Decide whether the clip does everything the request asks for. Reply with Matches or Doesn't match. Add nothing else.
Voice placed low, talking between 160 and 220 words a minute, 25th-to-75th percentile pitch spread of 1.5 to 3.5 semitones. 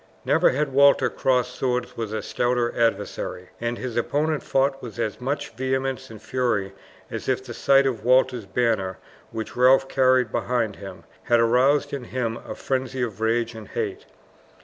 Matches